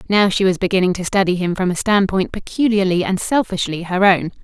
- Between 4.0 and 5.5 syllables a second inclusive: No, 5.8 syllables/s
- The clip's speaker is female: Yes, female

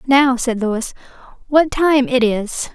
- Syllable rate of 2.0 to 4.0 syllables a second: Yes, 3.4 syllables/s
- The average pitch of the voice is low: No, very high, 255 Hz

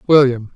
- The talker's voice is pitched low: Yes, low, 130 Hz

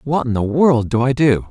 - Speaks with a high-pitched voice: No, low, 130 Hz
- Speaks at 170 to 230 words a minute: No, fast, 280 wpm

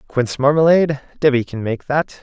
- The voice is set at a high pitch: No, medium, 140 Hz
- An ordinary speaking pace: Yes, average, 160 wpm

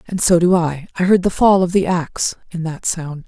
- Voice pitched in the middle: Yes, medium, 175 Hz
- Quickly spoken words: Yes, fast, 255 wpm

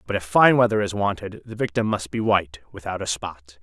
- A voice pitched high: No, low, 100 Hz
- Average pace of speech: No, fast, 230 wpm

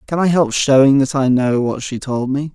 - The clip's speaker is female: No, male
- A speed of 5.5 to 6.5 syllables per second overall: No, 5.0 syllables/s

